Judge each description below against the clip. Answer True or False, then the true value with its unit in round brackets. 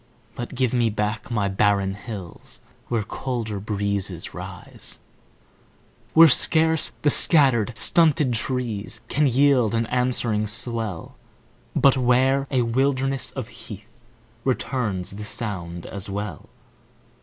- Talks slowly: True (115 wpm)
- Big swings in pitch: False (4.3 semitones)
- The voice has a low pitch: True (115 Hz)